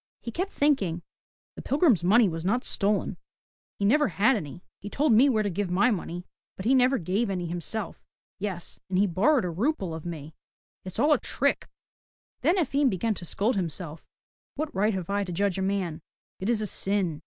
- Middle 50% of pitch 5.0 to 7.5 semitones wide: Yes, average, 5.3 semitones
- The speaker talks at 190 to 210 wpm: Yes, average, 200 wpm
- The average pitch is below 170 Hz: No, high, 200 Hz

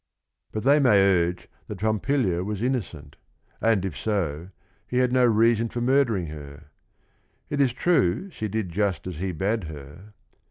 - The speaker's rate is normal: Yes, average, 160 wpm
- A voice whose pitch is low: Yes, low, 105 Hz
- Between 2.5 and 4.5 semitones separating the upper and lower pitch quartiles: No, wide, 5.6 semitones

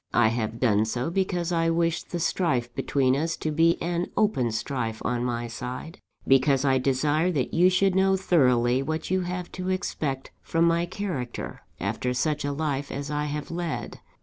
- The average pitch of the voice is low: No, medium, 150 Hz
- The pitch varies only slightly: No, average, 5.3 semitones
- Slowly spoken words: No, average, 180 wpm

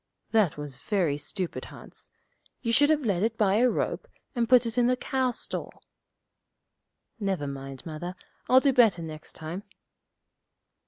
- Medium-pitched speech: No, high, 205 Hz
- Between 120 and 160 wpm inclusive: Yes, average, 155 wpm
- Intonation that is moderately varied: No, wide, 7.5 semitones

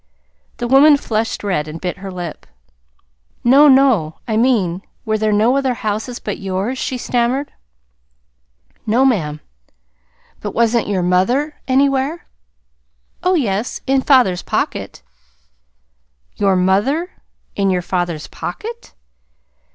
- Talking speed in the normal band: No, slow, 120 wpm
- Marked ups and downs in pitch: Yes, wide, 5.9 semitones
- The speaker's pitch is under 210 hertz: No, high, 225 Hz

